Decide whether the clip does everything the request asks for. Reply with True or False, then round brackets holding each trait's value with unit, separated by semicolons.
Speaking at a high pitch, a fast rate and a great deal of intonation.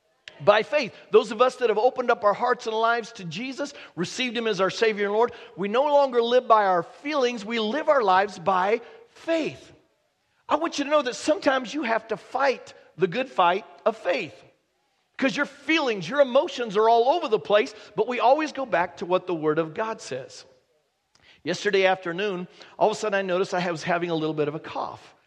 True (225 Hz; 215 wpm; 6.0 semitones)